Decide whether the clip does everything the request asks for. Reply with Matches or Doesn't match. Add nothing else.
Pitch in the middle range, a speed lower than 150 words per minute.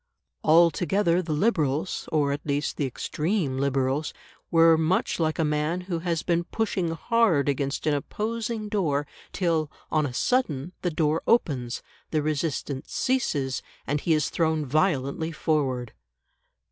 Matches